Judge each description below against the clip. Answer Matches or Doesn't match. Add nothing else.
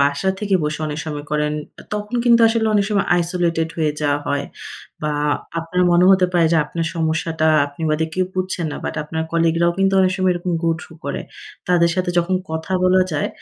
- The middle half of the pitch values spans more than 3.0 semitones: Doesn't match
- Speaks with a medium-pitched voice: Matches